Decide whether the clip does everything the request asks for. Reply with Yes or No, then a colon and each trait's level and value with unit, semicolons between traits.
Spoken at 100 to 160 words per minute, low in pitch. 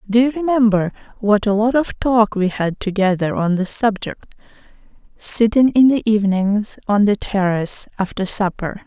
No: average, 155 wpm; high, 215 Hz